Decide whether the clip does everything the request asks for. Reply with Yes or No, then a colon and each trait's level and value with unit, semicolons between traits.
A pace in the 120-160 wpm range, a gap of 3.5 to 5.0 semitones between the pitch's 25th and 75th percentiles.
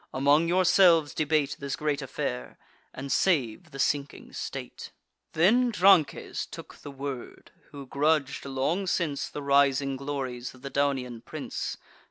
No: slow, 135 wpm; average, 2.8 semitones